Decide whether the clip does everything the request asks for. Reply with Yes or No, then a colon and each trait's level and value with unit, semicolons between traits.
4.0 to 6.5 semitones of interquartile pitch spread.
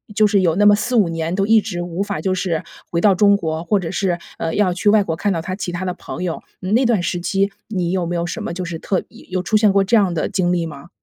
No: average, 2.8 semitones